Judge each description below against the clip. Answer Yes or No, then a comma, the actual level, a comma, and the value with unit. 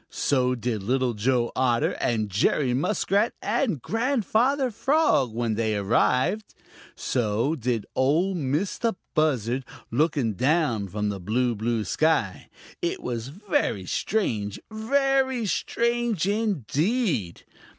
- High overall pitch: No, low, 135 Hz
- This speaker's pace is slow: Yes, slow, 110 wpm